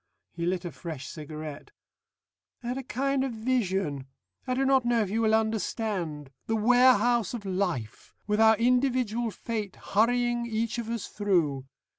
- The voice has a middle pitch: No, high, 220 Hz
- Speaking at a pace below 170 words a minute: Yes, average, 160 wpm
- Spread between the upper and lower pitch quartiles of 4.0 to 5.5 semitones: Yes, average, 4.8 semitones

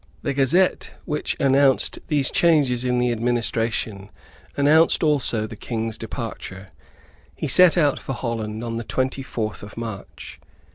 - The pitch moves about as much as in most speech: Yes, average, 3.9 semitones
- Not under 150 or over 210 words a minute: No, average, 140 wpm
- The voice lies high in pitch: No, low, 125 Hz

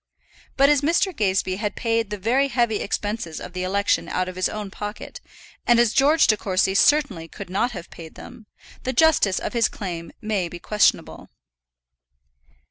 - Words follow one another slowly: No, average, 175 wpm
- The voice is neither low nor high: No, high, 210 Hz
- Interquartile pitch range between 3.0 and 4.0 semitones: No, average, 4.4 semitones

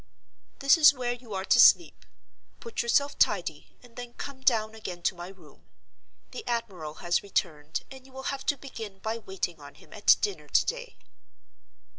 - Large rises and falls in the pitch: Yes, wide, 6.4 semitones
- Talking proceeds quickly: No, average, 180 wpm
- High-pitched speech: Yes, high, 230 Hz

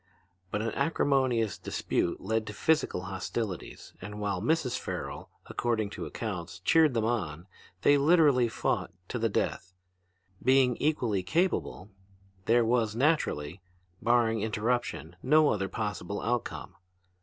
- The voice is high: No, low, 115 Hz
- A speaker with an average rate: No, slow, 125 wpm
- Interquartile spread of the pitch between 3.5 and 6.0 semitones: Yes, average, 4.3 semitones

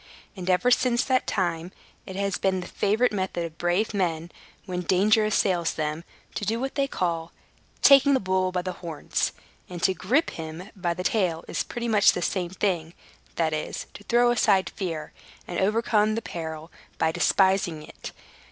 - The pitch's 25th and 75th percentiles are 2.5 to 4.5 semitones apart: Yes, average, 3.9 semitones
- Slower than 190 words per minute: Yes, average, 180 wpm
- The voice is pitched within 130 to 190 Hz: Yes, medium, 185 Hz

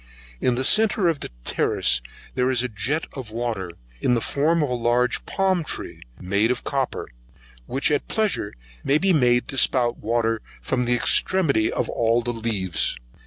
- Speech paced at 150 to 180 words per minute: Yes, average, 165 wpm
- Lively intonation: No, average, 4.1 semitones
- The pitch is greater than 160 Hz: No, low, 125 Hz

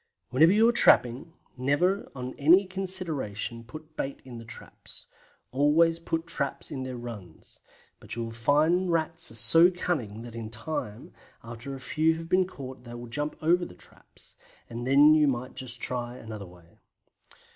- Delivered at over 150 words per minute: Yes, average, 165 wpm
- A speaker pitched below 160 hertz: Yes, low, 135 Hz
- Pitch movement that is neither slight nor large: No, wide, 5.7 semitones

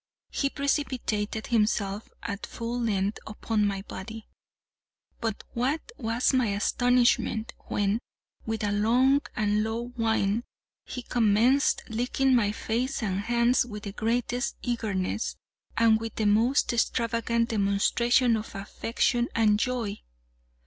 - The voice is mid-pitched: No, high, 225 Hz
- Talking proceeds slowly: Yes, slow, 120 wpm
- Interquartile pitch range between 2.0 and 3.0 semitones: Yes, narrow, 2.6 semitones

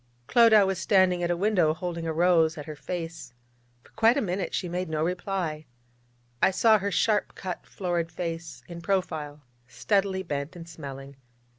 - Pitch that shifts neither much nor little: Yes, average, 3.1 semitones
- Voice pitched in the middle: Yes, medium, 175 Hz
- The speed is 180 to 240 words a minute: No, average, 170 wpm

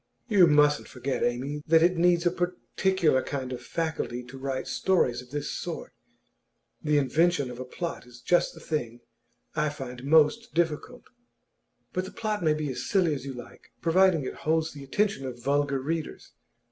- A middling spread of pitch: Yes, average, 4.7 semitones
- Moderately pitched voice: Yes, medium, 150 Hz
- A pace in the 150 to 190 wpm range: Yes, average, 175 wpm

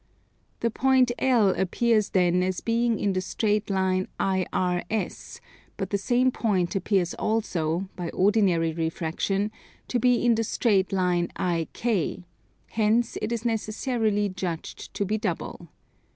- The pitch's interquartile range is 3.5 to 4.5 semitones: Yes, average, 3.8 semitones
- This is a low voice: No, high, 200 Hz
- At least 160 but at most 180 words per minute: No, slow, 135 wpm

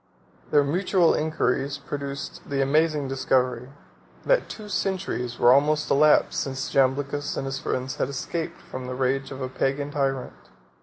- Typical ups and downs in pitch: No, narrow, 2.2 semitones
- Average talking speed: Yes, average, 150 wpm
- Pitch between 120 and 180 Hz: Yes, medium, 140 Hz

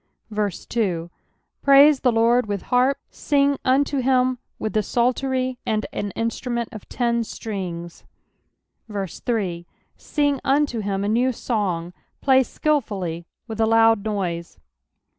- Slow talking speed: Yes, slow, 120 wpm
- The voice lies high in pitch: Yes, high, 230 Hz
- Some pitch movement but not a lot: Yes, average, 4.3 semitones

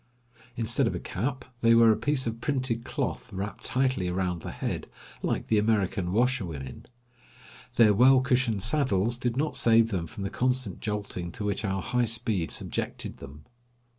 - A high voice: No, low, 115 Hz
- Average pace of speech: Yes, average, 165 wpm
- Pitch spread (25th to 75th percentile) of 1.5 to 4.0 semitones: No, average, 4.5 semitones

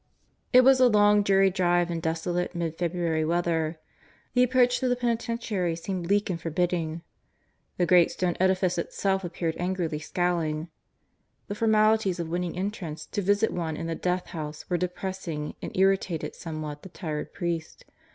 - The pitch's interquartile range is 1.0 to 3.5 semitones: Yes, average, 3.0 semitones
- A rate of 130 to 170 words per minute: Yes, average, 160 wpm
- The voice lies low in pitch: No, medium, 180 Hz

